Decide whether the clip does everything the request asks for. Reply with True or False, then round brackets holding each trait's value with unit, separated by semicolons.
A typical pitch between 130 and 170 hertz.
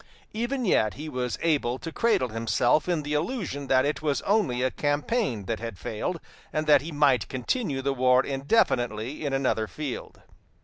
True (140 Hz)